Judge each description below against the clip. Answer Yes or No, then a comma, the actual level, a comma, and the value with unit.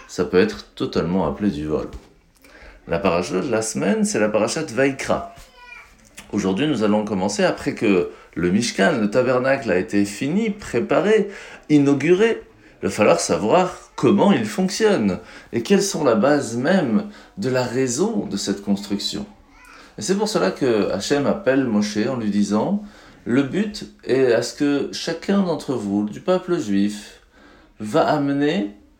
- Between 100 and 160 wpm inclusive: Yes, average, 155 wpm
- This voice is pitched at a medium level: No, low, 130 Hz